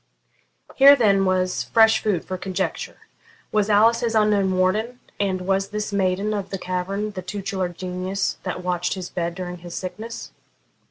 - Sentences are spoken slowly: No, average, 160 wpm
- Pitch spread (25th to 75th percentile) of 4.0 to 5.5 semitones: No, narrow, 2.5 semitones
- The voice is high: Yes, high, 195 Hz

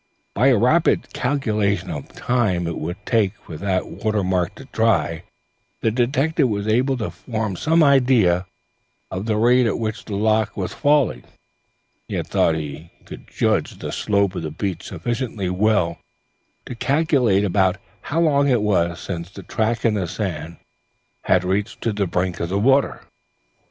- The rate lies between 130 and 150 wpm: No, average, 165 wpm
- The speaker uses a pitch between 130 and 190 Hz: No, low, 105 Hz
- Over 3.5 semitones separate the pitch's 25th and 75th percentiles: Yes, average, 5.1 semitones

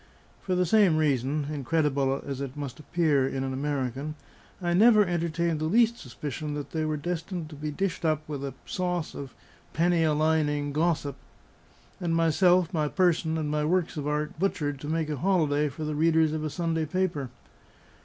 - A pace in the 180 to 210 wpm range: Yes, average, 185 wpm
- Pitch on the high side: No, medium, 155 Hz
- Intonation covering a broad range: No, average, 2.8 semitones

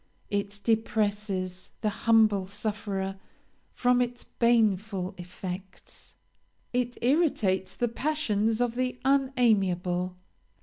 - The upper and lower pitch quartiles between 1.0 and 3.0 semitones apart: No, average, 4.1 semitones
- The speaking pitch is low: No, high, 215 Hz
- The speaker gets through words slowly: Yes, slow, 90 wpm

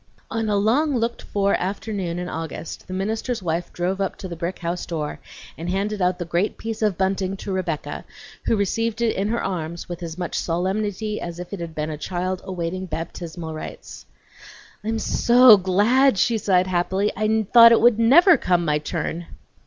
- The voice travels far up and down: No, average, 3.9 semitones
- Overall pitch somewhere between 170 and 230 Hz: Yes, high, 190 Hz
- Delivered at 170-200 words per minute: Yes, average, 190 wpm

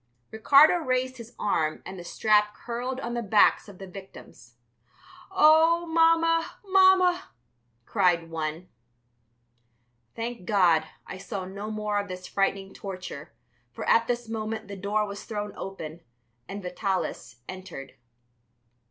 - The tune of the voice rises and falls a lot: No, average, 4.7 semitones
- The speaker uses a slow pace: Yes, slow, 130 wpm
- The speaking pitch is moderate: No, high, 210 Hz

